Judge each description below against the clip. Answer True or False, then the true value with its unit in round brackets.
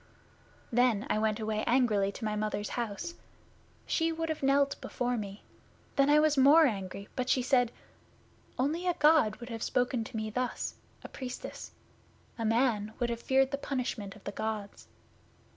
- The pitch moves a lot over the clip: False (4.2 semitones)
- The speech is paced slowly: False (170 wpm)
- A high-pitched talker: True (245 Hz)